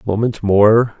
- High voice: No, low, 110 Hz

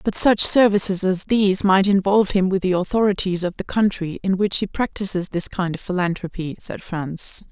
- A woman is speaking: Yes, female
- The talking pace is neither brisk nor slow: Yes, average, 190 wpm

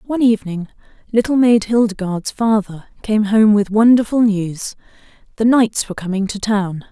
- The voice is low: No, high, 210 Hz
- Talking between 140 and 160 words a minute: Yes, average, 145 wpm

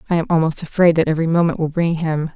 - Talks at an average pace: No, fast, 255 wpm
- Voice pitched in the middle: Yes, medium, 165 Hz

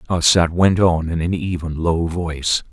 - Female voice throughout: No, male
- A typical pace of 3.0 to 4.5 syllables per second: Yes, 4.4 syllables/s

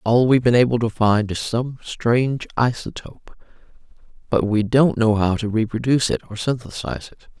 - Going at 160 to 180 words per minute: Yes, average, 170 wpm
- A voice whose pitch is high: No, low, 115 Hz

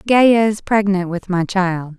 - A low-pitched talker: No, high, 195 Hz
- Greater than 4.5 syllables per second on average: No, 3.9 syllables/s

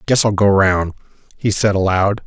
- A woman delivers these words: No, male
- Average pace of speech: Yes, average, 185 wpm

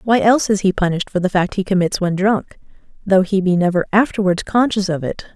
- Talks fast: Yes, fast, 225 wpm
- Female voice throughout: Yes, female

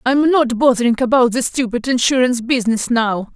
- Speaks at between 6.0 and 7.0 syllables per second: No, 5.5 syllables/s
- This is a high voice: Yes, high, 245 Hz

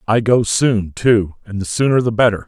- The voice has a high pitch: No, low, 110 Hz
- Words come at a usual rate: No, fast, 220 wpm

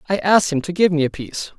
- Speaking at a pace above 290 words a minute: Yes, fast, 300 wpm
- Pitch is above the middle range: No, medium, 165 Hz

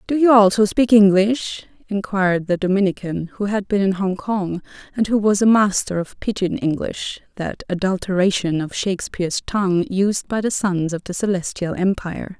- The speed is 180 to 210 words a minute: No, average, 165 wpm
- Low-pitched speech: No, high, 195 Hz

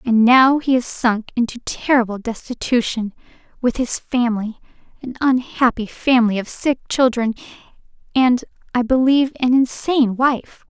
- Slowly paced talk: Yes, slow, 125 wpm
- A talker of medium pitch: No, high, 245 Hz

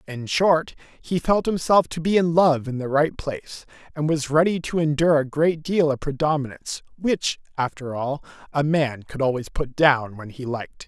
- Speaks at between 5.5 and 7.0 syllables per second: No, 4.9 syllables/s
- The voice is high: No, medium, 150 Hz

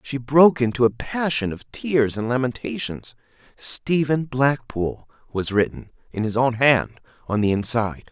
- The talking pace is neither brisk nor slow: Yes, average, 150 wpm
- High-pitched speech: No, low, 125 Hz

